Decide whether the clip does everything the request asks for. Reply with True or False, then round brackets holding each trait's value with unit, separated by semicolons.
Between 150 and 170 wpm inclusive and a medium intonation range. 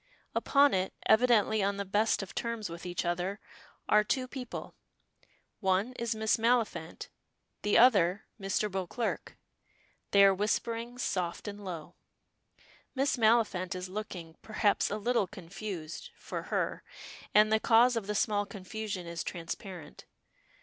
False (135 wpm; 3.4 semitones)